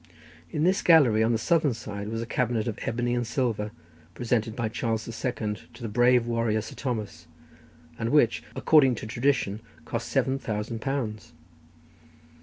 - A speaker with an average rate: Yes, average, 165 wpm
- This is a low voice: Yes, low, 115 Hz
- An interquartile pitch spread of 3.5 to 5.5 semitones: No, narrow, 2.5 semitones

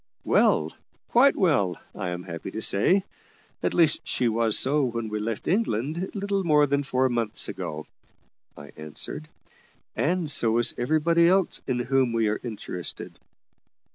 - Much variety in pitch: Yes, wide, 7.1 semitones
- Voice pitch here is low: Yes, low, 125 Hz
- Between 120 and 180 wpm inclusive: Yes, average, 150 wpm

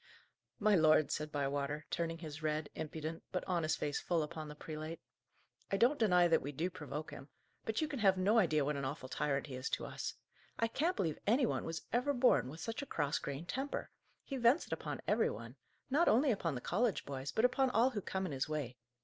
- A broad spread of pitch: Yes, wide, 7.0 semitones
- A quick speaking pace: Yes, fast, 225 wpm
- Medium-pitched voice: Yes, medium, 165 Hz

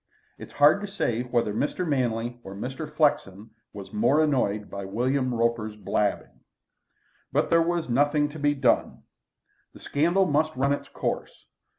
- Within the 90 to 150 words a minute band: No, average, 160 wpm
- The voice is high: No, low, 130 Hz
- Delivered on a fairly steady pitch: No, average, 5.0 semitones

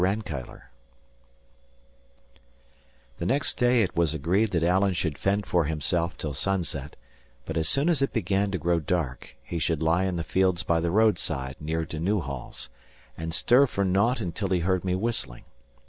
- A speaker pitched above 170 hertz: No, very low, 90 Hz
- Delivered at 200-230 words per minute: No, average, 170 wpm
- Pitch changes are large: No, average, 3.6 semitones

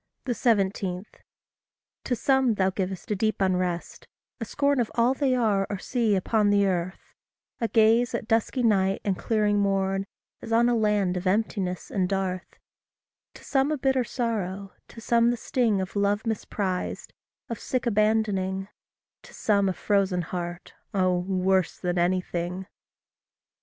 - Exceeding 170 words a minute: No, average, 150 wpm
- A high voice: Yes, high, 200 Hz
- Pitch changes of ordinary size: Yes, average, 3.4 semitones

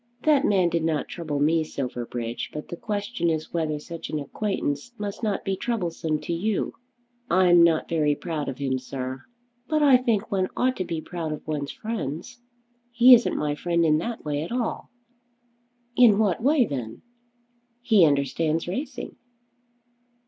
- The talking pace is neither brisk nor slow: Yes, average, 165 wpm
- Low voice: No, medium, 170 Hz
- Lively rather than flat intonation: Yes, wide, 6.4 semitones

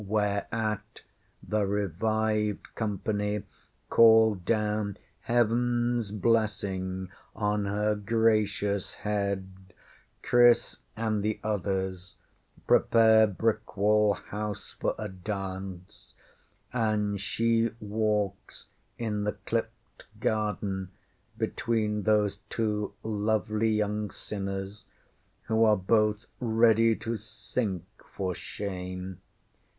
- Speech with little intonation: Yes, narrow, 1.8 semitones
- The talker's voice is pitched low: Yes, low, 105 Hz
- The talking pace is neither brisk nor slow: No, slow, 85 wpm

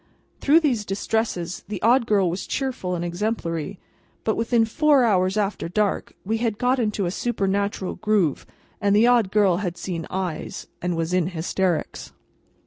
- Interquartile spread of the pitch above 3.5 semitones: Yes, average, 3.9 semitones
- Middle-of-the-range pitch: No, high, 200 Hz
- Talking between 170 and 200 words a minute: No, average, 160 wpm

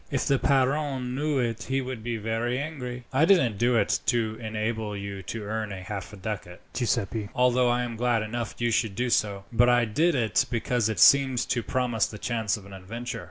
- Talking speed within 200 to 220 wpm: Yes, fast, 205 wpm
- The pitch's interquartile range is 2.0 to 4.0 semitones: Yes, average, 2.8 semitones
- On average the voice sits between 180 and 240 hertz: No, low, 120 Hz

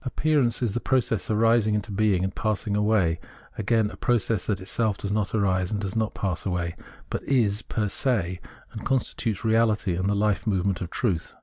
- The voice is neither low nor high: No, low, 105 Hz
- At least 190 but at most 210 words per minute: Yes, average, 195 wpm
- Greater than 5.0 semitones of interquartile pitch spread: No, average, 2.8 semitones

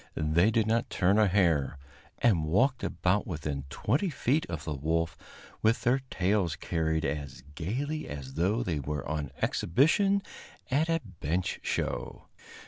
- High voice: No, very low, 90 Hz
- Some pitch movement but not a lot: No, wide, 7.0 semitones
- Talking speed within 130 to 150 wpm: Yes, average, 145 wpm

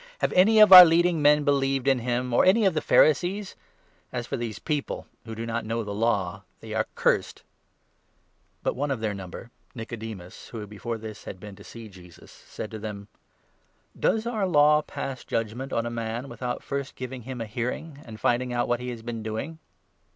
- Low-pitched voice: Yes, low, 120 Hz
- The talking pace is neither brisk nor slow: No, fast, 215 wpm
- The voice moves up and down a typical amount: Yes, average, 4.8 semitones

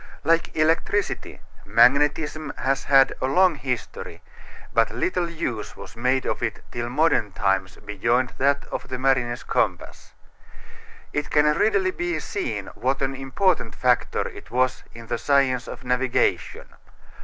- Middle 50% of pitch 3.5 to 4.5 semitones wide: Yes, average, 4.2 semitones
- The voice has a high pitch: No, low, 135 Hz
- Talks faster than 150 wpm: No, average, 140 wpm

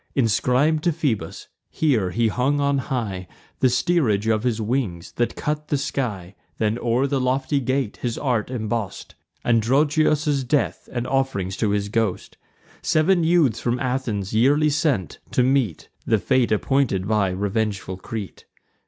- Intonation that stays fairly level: No, average, 4.5 semitones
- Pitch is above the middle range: No, low, 125 Hz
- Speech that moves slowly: No, average, 145 wpm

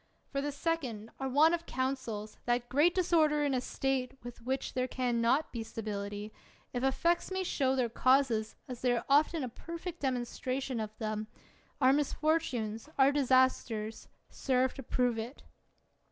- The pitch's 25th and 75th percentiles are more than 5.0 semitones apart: No, average, 3.5 semitones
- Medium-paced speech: Yes, average, 160 wpm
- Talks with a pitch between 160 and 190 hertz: No, very high, 260 Hz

